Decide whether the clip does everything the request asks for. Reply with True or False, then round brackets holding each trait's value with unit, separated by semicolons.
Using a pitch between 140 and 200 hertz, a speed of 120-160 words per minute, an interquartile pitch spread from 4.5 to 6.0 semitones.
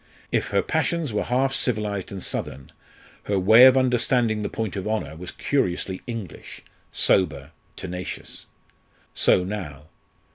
False (105 Hz; 135 wpm; 5.0 semitones)